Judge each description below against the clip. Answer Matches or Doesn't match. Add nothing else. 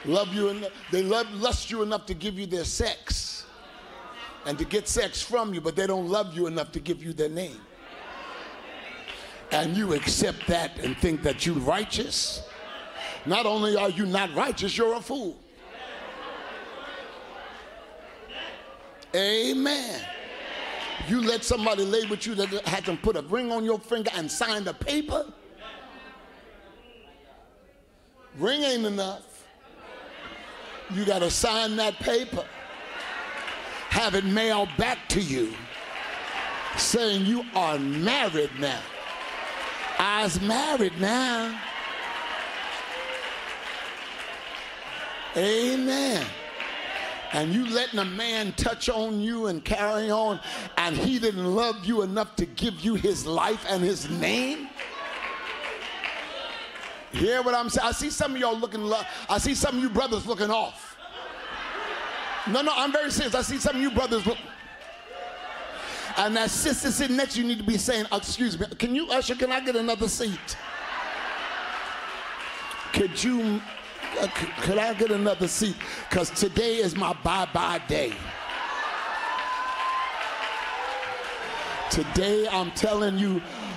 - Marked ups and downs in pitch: Doesn't match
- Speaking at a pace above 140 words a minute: Doesn't match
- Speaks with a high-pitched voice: Matches